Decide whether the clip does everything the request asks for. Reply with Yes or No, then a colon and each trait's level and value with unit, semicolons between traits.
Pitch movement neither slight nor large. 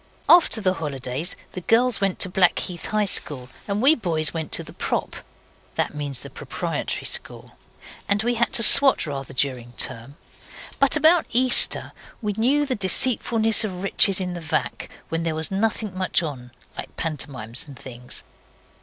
No: wide, 7.5 semitones